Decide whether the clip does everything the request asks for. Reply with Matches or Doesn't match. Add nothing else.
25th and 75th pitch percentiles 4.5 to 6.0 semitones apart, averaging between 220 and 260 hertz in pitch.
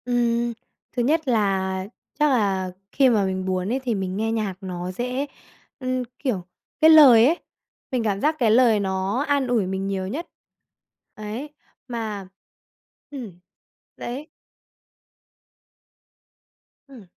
Matches